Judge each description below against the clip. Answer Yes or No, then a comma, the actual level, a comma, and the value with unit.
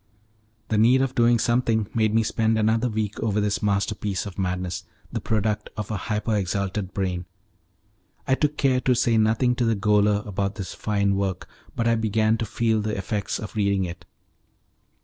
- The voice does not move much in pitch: Yes, narrow, 2.3 semitones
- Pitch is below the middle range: Yes, low, 105 Hz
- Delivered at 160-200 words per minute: Yes, average, 180 wpm